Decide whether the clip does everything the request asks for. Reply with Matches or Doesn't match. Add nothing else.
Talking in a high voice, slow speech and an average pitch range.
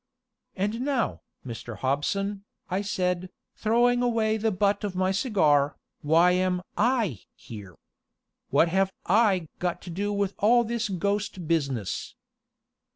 Matches